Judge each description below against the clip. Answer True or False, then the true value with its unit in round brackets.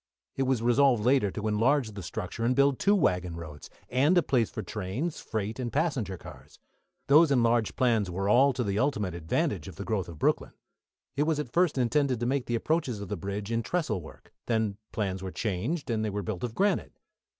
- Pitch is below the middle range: True (115 Hz)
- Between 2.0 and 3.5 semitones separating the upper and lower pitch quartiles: False (5.4 semitones)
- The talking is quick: True (210 wpm)